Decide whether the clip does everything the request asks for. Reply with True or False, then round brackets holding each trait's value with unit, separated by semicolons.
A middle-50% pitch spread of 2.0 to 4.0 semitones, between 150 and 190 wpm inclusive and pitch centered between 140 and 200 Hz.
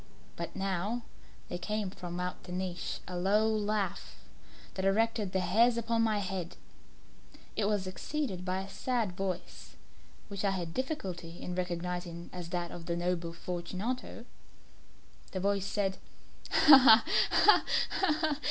False (3.5 semitones; 140 wpm; 190 Hz)